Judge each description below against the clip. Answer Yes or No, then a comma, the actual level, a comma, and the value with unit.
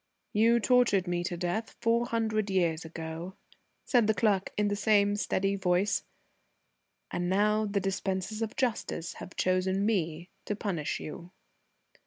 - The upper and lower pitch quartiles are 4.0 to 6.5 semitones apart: No, average, 3.3 semitones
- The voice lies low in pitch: No, high, 195 Hz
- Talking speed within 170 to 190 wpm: No, average, 145 wpm